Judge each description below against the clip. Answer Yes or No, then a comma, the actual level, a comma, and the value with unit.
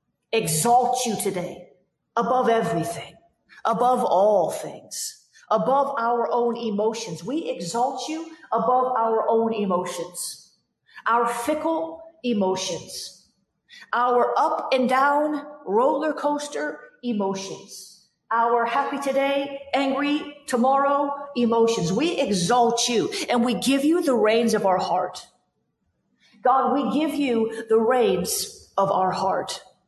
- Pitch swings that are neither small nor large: Yes, average, 4.0 semitones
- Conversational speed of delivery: No, slow, 110 wpm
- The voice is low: No, high, 245 Hz